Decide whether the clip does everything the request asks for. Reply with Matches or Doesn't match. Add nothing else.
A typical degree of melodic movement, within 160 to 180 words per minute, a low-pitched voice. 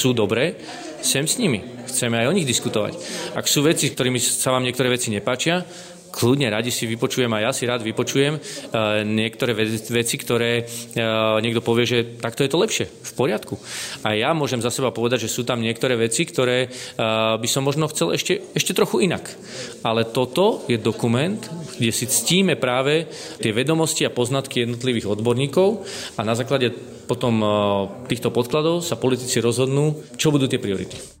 Matches